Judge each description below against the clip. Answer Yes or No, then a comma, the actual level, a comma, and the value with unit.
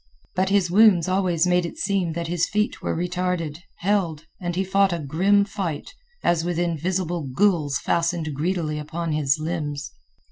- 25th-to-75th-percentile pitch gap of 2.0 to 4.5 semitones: Yes, average, 2.9 semitones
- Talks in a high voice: No, medium, 175 Hz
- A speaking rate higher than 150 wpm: Yes, average, 165 wpm